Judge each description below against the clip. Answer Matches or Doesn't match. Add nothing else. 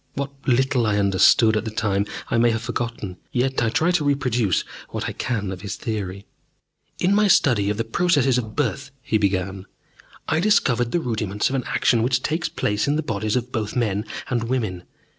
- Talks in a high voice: Doesn't match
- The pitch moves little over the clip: Doesn't match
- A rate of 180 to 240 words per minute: Matches